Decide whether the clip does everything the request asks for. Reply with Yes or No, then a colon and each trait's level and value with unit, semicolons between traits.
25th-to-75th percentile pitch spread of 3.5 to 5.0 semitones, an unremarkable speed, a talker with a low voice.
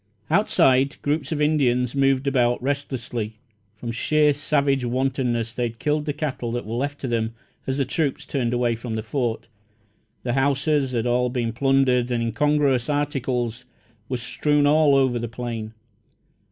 No: average, 3.1 semitones; average, 160 wpm; low, 130 Hz